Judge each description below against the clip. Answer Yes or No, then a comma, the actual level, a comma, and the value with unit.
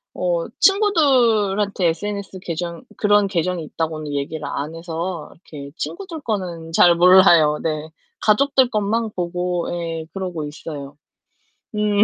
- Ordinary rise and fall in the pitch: Yes, average, 4.4 semitones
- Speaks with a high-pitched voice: No, medium, 180 Hz